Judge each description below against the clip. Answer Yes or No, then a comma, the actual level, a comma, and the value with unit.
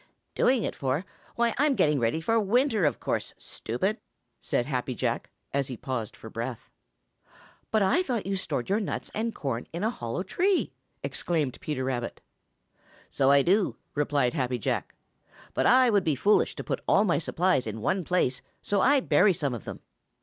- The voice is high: No, medium, 165 Hz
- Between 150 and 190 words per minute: Yes, average, 180 wpm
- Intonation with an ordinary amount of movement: No, wide, 8.6 semitones